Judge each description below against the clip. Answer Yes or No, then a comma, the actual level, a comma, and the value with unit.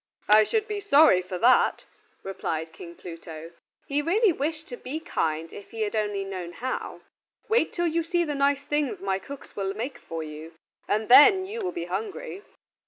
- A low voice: No, very high, 255 Hz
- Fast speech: No, average, 185 wpm